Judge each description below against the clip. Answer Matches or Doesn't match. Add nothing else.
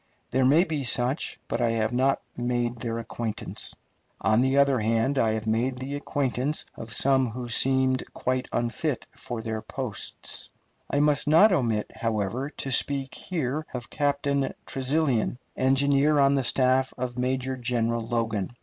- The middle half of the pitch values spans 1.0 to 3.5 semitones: Matches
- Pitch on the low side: Matches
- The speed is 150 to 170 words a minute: Matches